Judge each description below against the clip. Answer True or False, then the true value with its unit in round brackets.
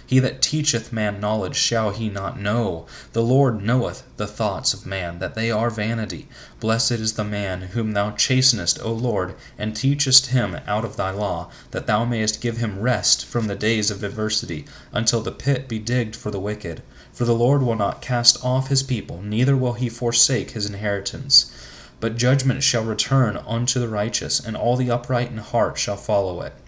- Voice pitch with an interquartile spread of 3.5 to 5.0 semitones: False (2.9 semitones)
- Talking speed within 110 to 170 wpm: False (195 wpm)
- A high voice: False (115 Hz)